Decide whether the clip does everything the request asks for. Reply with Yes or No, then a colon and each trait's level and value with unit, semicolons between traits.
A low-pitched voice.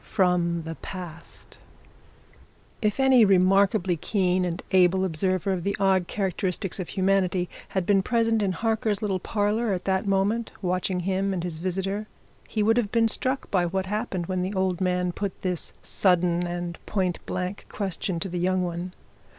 No: high, 190 Hz